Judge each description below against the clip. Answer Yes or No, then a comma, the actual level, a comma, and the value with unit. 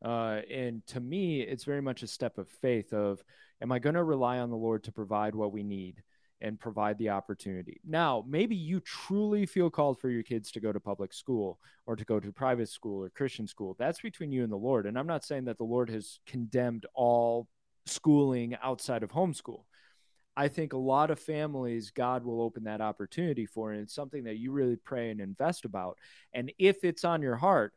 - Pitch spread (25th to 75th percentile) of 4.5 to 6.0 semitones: Yes, average, 5.0 semitones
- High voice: No, low, 125 Hz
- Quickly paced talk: Yes, fast, 215 wpm